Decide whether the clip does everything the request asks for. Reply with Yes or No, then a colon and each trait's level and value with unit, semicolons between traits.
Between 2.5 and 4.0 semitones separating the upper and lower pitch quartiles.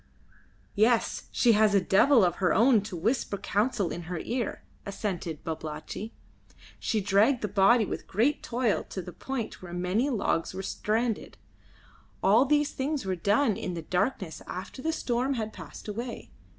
No: average, 4.5 semitones